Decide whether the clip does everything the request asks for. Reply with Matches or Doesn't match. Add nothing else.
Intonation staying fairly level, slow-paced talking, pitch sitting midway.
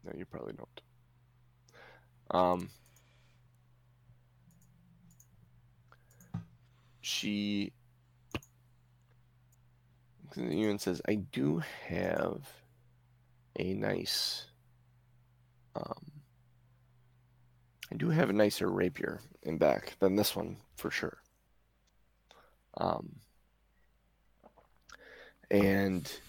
Doesn't match